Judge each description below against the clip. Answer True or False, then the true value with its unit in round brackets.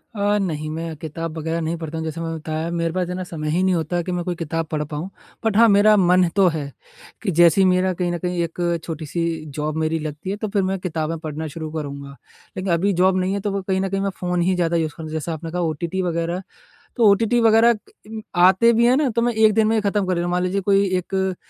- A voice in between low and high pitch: True (175 Hz)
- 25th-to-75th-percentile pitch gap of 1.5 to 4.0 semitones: True (3.2 semitones)